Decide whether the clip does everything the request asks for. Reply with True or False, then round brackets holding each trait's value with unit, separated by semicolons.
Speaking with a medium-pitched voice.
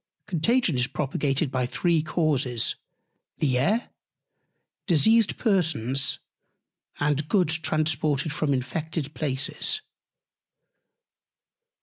True (155 Hz)